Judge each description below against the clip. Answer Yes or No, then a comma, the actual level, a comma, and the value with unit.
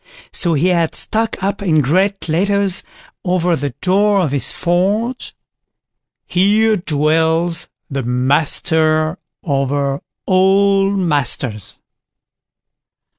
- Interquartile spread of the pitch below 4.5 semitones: No, average, 4.9 semitones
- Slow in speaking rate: Yes, slow, 95 wpm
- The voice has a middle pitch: Yes, medium, 170 Hz